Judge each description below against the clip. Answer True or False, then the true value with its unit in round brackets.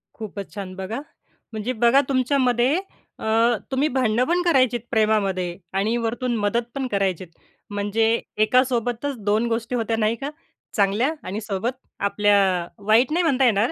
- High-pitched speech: True (230 Hz)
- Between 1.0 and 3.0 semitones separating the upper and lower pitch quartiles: False (3.7 semitones)